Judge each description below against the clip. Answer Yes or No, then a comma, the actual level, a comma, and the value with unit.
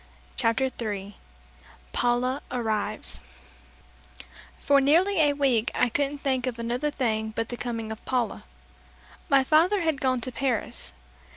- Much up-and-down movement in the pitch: No, average, 3.5 semitones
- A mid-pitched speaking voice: No, very high, 255 Hz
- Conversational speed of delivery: No, slow, 130 wpm